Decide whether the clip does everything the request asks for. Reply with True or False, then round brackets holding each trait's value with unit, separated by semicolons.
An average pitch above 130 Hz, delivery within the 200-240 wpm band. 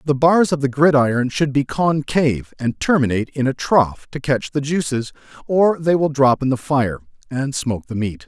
True (140 Hz; 205 wpm)